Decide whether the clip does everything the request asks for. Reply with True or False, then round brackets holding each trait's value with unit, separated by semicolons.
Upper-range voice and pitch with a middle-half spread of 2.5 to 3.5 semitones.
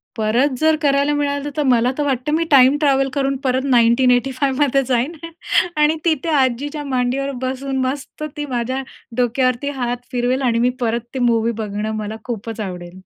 True (260 Hz; 2.9 semitones)